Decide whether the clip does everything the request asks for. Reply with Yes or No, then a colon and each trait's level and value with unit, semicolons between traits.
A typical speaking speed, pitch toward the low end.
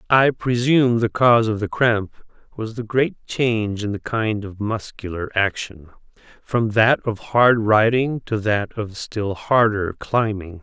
Yes: average, 160 wpm; low, 110 Hz